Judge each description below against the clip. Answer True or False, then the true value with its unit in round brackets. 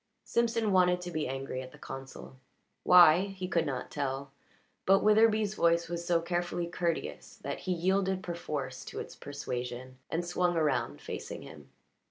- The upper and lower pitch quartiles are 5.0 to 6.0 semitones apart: True (5.3 semitones)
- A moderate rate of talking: True (160 wpm)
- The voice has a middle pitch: True (170 Hz)